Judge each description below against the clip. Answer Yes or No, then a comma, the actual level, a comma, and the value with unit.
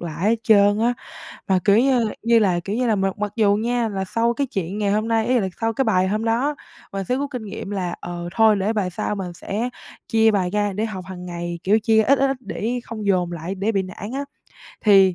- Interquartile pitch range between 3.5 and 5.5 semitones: No, average, 3.1 semitones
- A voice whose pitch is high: Yes, high, 210 Hz